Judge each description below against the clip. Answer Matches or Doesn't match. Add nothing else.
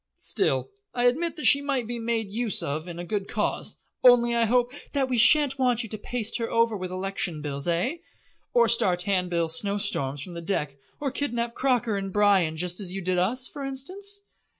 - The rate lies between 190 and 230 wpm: Matches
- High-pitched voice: Matches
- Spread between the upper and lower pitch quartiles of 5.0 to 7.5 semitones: Matches